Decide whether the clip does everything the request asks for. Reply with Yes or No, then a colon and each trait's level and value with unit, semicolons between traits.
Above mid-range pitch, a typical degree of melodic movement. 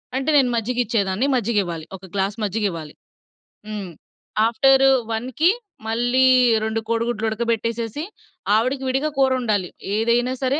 Yes: high, 230 Hz; average, 3.5 semitones